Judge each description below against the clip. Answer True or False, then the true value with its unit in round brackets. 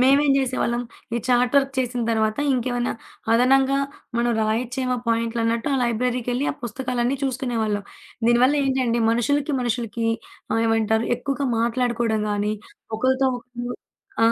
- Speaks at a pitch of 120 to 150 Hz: False (245 Hz)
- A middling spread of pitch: False (2.1 semitones)